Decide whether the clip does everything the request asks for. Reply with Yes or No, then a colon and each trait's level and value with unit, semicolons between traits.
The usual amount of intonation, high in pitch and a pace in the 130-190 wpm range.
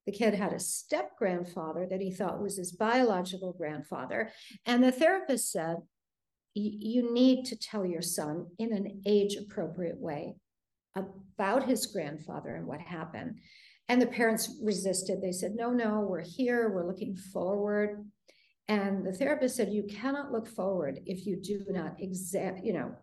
Yes: average, 3.4 semitones; high, 205 Hz; average, 160 wpm